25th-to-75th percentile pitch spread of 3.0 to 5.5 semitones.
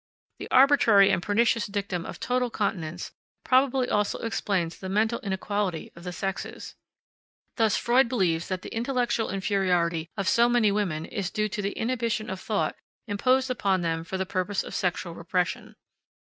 Yes: average, 4.2 semitones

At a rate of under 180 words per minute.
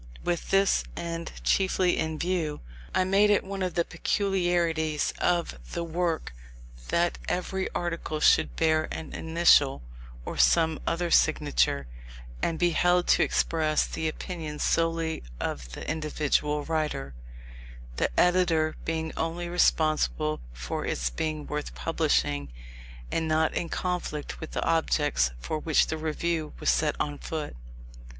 Yes: slow, 135 wpm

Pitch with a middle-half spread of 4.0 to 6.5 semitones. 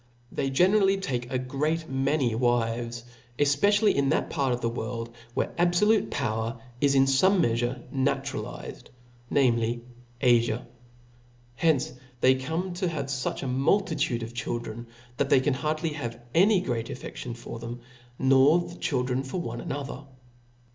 Yes: average, 4.6 semitones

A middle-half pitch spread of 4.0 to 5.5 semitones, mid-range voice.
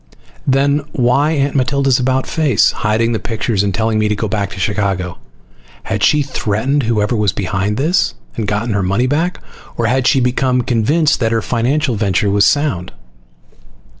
No: average, 4.6 semitones; low, 115 Hz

